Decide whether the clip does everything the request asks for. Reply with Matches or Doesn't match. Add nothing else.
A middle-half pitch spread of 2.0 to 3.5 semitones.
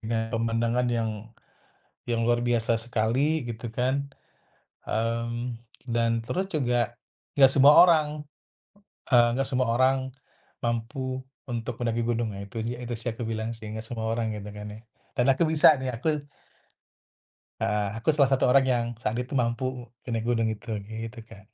Matches